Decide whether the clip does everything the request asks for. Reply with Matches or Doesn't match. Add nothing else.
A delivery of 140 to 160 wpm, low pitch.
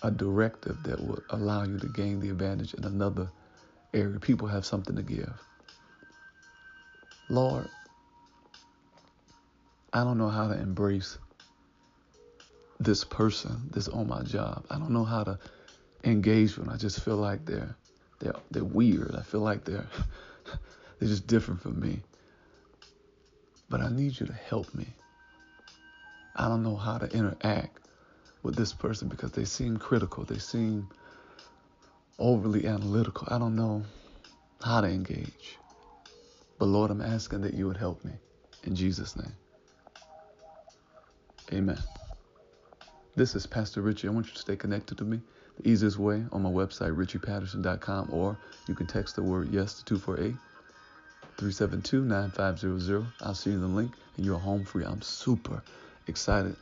Matches